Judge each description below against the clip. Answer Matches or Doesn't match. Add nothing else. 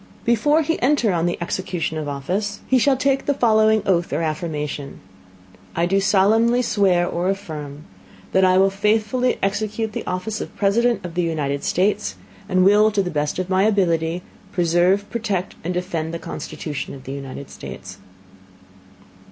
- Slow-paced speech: Doesn't match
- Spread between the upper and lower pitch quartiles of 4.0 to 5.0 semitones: Matches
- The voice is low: Doesn't match